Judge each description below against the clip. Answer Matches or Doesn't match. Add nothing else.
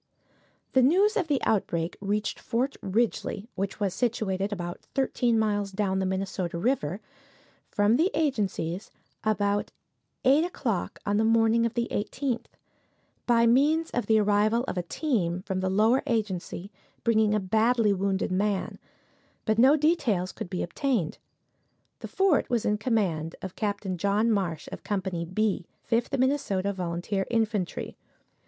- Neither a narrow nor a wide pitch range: Matches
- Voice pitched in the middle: Doesn't match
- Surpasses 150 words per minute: Doesn't match